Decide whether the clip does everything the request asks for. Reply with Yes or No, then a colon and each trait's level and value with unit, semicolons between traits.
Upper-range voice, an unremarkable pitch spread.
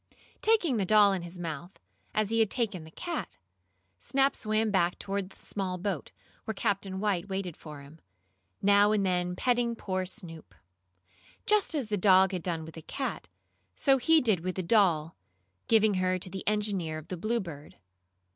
Yes: high, 195 Hz; average, 3.5 semitones